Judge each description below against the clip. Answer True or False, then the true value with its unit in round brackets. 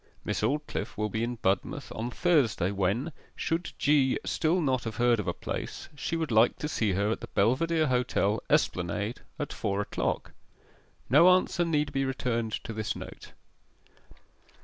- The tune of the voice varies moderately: False (5.8 semitones)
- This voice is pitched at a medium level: False (120 Hz)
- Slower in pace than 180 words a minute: True (165 wpm)